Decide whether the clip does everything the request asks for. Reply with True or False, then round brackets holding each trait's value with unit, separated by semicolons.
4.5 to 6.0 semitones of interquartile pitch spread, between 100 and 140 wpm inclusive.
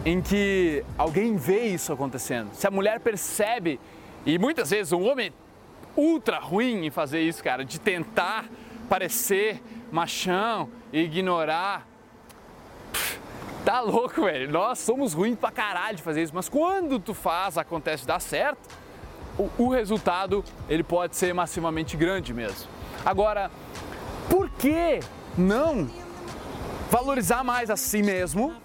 True (5.3 semitones; 135 wpm)